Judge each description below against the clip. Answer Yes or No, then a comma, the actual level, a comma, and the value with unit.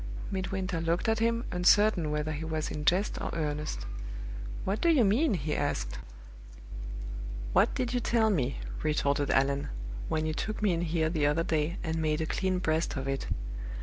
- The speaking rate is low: No, average, 180 wpm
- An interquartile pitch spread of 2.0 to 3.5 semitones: No, average, 4.4 semitones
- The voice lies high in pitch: No, medium, 165 Hz